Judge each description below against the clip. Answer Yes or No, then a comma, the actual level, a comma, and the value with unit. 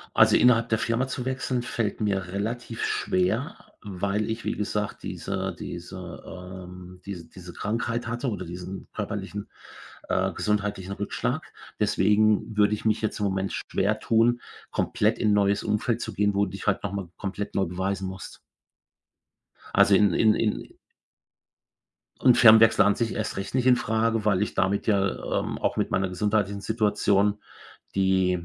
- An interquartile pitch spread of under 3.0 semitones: Yes, narrow, 2.5 semitones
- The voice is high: No, low, 105 Hz